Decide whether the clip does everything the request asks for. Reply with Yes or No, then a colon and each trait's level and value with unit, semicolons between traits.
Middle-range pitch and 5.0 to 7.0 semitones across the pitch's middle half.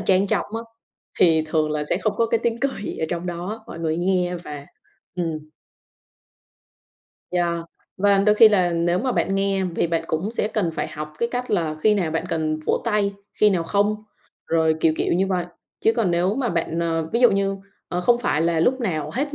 No: medium, 180 Hz; average, 4.4 semitones